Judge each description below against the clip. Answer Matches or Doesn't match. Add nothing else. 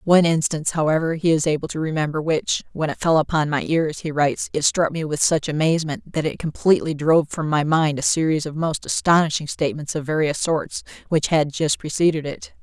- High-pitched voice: Doesn't match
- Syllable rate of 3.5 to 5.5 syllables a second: Doesn't match